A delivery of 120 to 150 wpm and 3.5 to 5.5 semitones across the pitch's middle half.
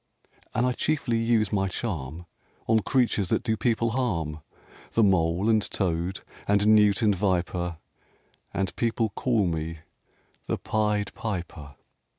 Yes: slow, 135 wpm; average, 4.4 semitones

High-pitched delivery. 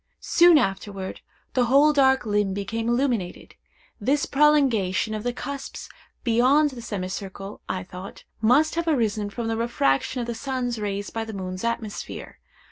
Yes: high, 230 Hz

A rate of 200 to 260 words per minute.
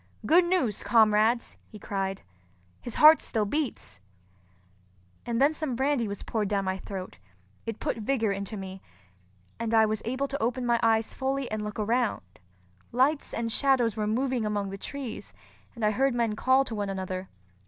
No: average, 170 wpm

